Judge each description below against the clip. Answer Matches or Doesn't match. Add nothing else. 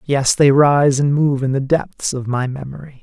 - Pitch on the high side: Doesn't match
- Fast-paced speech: Matches